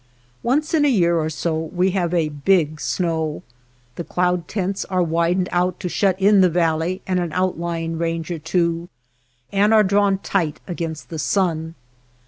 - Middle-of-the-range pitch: Yes, medium, 175 Hz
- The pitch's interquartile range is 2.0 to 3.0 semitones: Yes, narrow, 2.4 semitones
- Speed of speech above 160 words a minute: Yes, average, 175 wpm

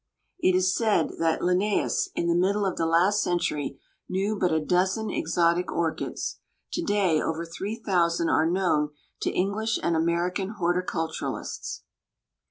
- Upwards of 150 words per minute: No, average, 145 wpm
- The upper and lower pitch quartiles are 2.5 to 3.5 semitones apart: Yes, average, 3.0 semitones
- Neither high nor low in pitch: Yes, medium, 180 Hz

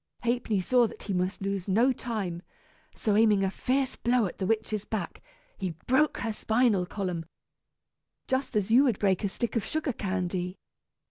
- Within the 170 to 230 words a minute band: Yes, average, 175 wpm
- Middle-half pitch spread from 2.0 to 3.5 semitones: No, average, 4.1 semitones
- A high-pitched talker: Yes, high, 210 Hz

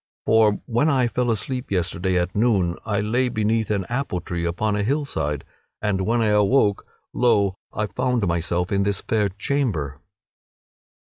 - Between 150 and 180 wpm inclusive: Yes, average, 155 wpm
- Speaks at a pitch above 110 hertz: No, low, 105 Hz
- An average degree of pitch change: Yes, average, 4.5 semitones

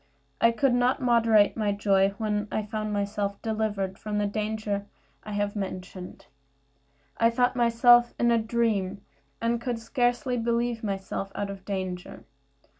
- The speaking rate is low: No, average, 145 wpm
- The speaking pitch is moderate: No, high, 215 Hz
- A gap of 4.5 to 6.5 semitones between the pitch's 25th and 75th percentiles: No, average, 2.7 semitones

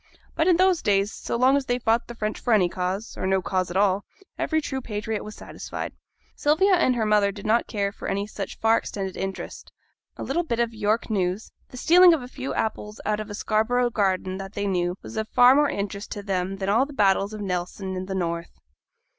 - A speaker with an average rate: No, fast, 230 wpm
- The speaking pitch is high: Yes, high, 210 Hz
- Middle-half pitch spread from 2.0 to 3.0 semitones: No, average, 4.0 semitones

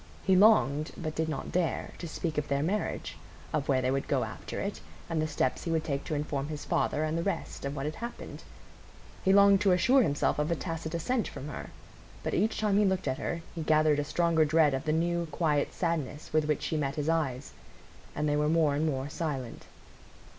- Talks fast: Yes, fast, 225 wpm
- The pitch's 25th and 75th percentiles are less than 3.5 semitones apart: Yes, average, 2.7 semitones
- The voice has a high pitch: No, medium, 155 Hz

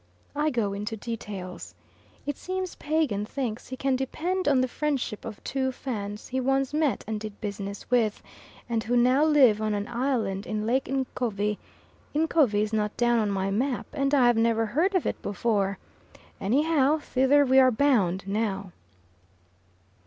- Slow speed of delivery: No, average, 165 wpm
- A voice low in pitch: No, high, 240 Hz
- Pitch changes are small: No, average, 4.7 semitones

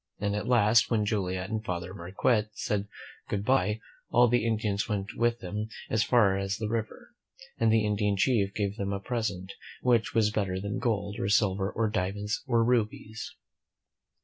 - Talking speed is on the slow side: No, average, 175 wpm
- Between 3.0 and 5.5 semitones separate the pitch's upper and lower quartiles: No, narrow, 2.4 semitones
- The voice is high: No, low, 105 Hz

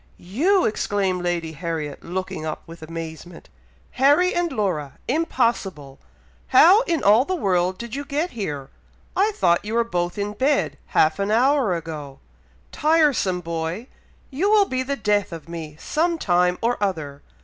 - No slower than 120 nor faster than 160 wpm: Yes, average, 155 wpm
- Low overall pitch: No, high, 200 Hz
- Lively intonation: Yes, wide, 8.6 semitones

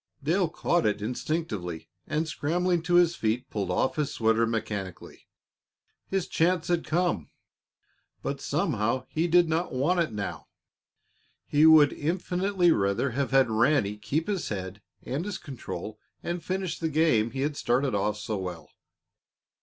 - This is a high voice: No, medium, 145 Hz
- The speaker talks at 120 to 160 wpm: Yes, average, 150 wpm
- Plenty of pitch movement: Yes, wide, 7.8 semitones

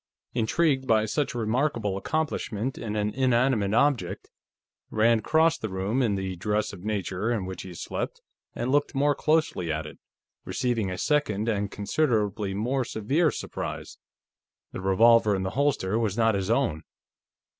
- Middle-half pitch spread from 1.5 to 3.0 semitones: No, average, 5.0 semitones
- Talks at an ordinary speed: Yes, average, 155 wpm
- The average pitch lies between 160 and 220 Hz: No, low, 110 Hz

